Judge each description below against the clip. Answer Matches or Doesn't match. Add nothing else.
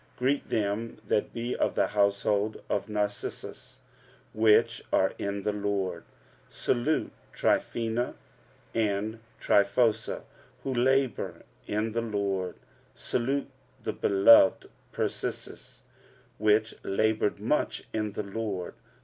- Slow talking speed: Matches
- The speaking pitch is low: Matches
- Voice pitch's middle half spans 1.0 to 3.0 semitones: Matches